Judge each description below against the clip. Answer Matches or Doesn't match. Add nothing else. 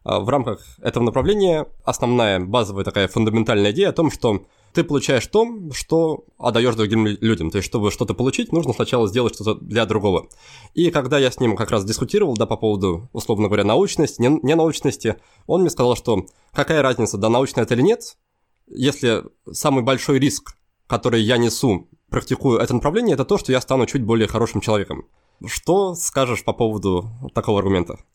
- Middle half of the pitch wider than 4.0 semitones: Matches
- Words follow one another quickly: Matches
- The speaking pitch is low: Matches